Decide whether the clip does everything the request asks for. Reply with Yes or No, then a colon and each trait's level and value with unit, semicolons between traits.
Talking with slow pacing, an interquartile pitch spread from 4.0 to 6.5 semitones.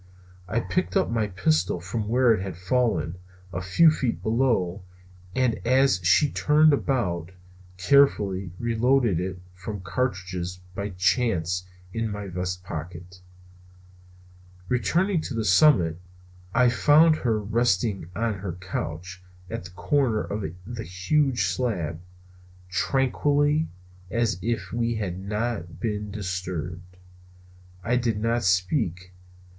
Yes: slow, 125 wpm; average, 5.1 semitones